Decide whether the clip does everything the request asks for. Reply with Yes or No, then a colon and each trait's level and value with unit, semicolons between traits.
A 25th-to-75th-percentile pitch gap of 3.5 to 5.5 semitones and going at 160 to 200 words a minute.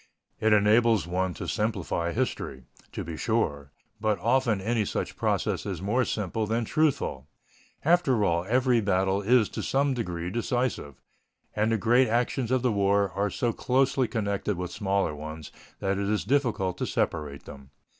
Yes: average, 4.5 semitones; average, 165 wpm